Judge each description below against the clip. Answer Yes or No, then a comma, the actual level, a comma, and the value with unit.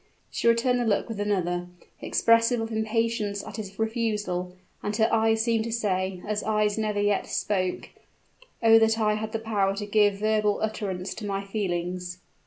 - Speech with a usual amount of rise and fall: No, narrow, 2.1 semitones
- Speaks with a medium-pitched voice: No, high, 210 Hz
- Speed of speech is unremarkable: Yes, average, 175 wpm